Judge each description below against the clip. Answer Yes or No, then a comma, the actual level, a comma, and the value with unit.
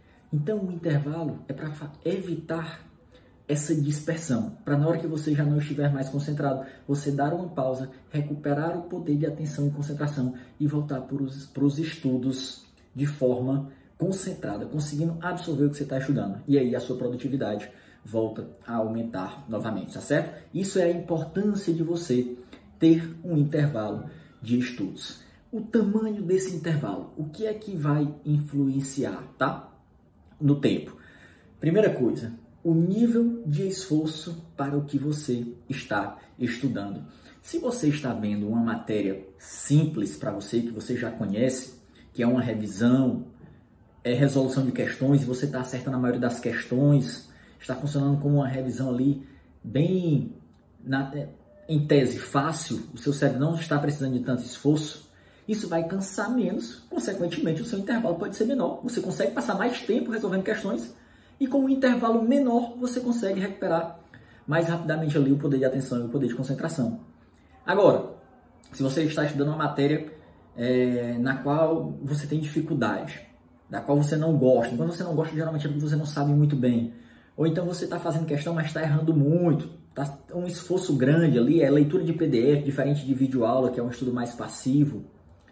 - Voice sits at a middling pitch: Yes, medium, 145 Hz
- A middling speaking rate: Yes, average, 165 wpm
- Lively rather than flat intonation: No, average, 4.3 semitones